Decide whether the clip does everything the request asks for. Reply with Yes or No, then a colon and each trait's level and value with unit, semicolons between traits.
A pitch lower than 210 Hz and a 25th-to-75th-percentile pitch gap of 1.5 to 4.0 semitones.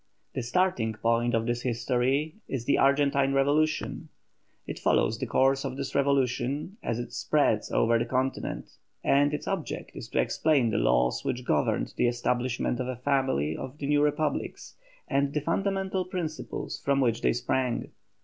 Yes: low, 135 Hz; average, 3.3 semitones